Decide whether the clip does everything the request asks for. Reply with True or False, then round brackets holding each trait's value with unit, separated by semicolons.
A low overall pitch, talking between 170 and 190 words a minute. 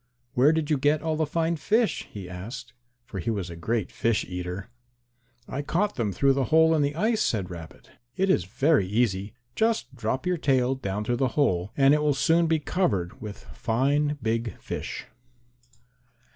True (130 Hz; 185 wpm)